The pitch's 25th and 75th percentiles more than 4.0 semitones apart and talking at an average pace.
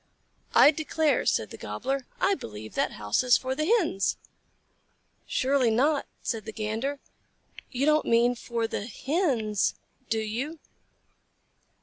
No: average, 5.0 semitones; slow, 130 wpm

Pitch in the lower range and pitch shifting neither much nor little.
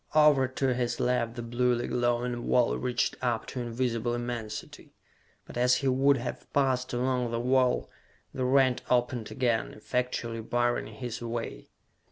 No: low, 125 Hz; narrow, 1.2 semitones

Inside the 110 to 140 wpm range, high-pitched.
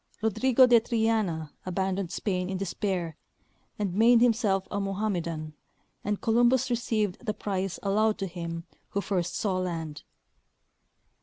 Yes: slow, 135 wpm; high, 195 Hz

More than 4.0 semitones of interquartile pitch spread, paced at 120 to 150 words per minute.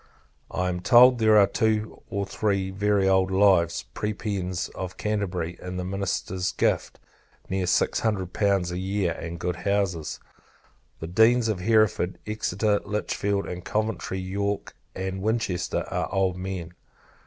No: narrow, 2.5 semitones; average, 140 wpm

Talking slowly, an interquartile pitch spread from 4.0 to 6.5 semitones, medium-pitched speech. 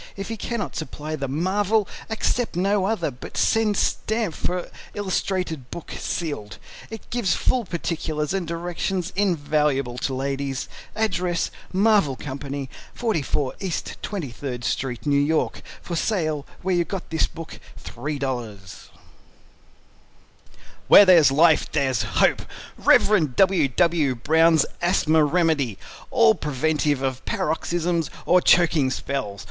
Yes: slow, 120 wpm; average, 5.1 semitones; medium, 160 Hz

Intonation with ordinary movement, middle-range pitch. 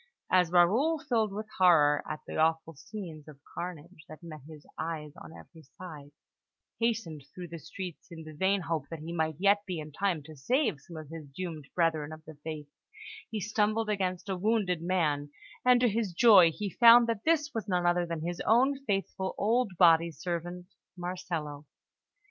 Yes: average, 4.4 semitones; medium, 175 Hz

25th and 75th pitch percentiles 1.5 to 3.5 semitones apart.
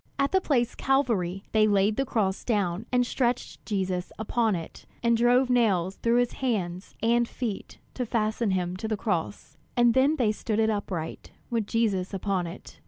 No: average, 3.9 semitones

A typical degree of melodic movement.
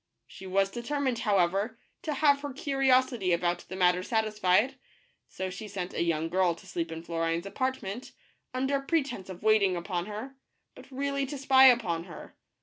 No: wide, 6.6 semitones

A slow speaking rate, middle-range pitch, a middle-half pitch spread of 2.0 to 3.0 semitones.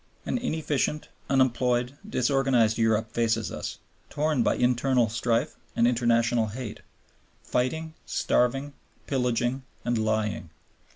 No: slow, 105 wpm; low, 125 Hz; average, 2.7 semitones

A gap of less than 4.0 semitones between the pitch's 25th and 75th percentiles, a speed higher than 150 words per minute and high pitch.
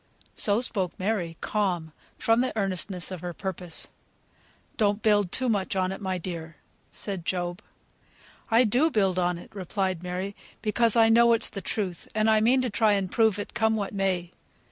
Yes: average, 3.5 semitones; average, 180 wpm; high, 195 Hz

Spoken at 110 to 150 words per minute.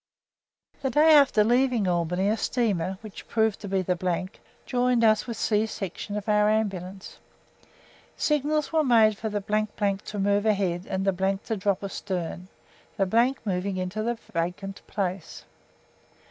Yes: average, 145 wpm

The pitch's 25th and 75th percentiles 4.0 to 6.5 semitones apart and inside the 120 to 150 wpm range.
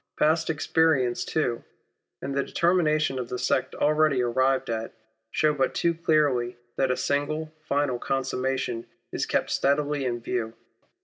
No: average, 3.4 semitones; average, 140 wpm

